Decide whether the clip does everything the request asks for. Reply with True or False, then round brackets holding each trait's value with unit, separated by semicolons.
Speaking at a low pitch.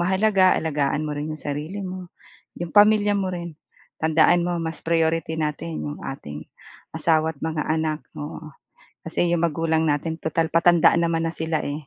False (160 Hz)